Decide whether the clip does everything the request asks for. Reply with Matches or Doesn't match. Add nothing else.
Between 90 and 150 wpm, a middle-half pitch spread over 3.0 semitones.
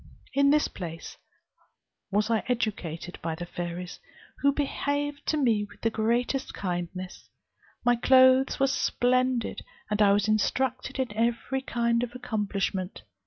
Matches